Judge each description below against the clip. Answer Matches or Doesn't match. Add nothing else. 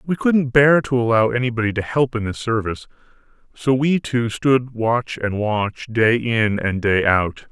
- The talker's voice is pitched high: Doesn't match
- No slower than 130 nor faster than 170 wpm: Doesn't match